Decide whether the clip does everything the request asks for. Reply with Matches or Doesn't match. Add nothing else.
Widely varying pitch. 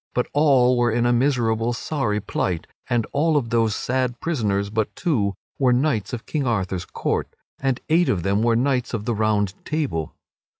Doesn't match